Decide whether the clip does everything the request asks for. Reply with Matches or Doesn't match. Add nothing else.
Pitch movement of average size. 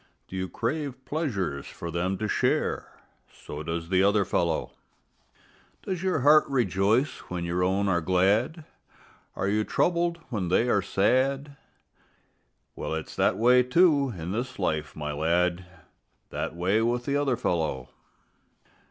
Doesn't match